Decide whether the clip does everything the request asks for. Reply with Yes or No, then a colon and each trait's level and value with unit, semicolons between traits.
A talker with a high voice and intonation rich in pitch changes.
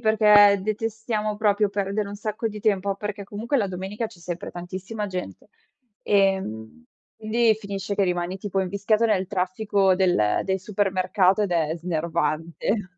No: high, 200 Hz; narrow, 2.5 semitones